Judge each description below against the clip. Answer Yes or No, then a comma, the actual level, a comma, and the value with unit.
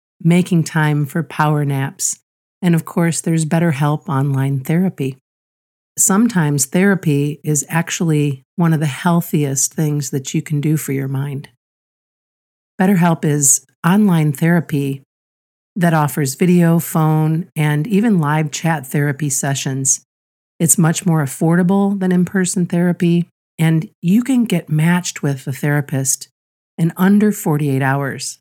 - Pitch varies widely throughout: No, average, 3.6 semitones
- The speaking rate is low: Yes, slow, 130 wpm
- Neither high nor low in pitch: Yes, medium, 155 Hz